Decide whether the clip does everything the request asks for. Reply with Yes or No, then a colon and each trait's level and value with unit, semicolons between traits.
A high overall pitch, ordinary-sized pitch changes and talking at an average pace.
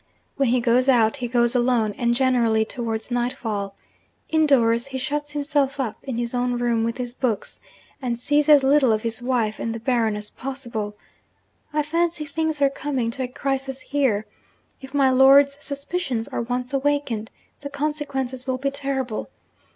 Yes: very high, 255 Hz; average, 3.2 semitones; average, 170 wpm